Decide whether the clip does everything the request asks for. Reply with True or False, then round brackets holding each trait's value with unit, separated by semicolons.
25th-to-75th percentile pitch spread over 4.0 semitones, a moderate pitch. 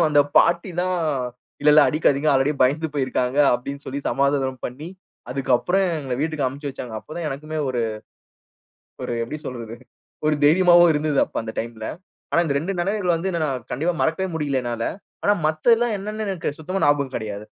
True (4.4 semitones; 150 Hz)